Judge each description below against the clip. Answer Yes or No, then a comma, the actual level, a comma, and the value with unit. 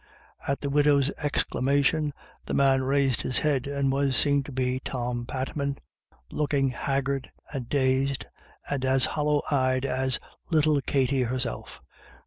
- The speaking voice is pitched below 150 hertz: Yes, low, 135 Hz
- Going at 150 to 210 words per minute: No, slow, 135 wpm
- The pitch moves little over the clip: Yes, narrow, 1.5 semitones